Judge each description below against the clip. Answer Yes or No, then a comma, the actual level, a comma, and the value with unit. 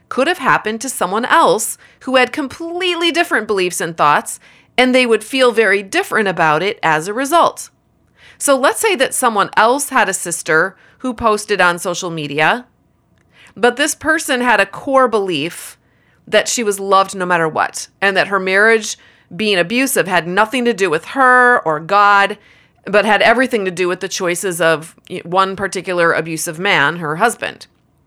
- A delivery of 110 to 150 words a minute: No, average, 175 wpm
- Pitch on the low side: No, high, 210 Hz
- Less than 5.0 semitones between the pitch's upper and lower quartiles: No, wide, 5.5 semitones